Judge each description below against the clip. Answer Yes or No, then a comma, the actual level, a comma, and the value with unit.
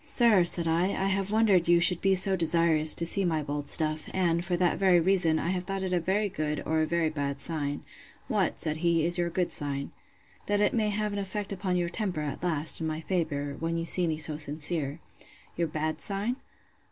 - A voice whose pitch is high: No, medium, 170 Hz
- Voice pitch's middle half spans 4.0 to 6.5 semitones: No, average, 3.4 semitones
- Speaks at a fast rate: Yes, fast, 220 wpm